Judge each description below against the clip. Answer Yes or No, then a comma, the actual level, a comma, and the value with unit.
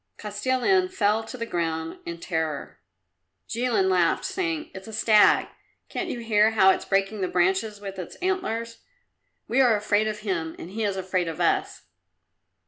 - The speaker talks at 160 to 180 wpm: Yes, average, 165 wpm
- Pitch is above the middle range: Yes, high, 210 Hz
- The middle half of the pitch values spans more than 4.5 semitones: No, average, 3.7 semitones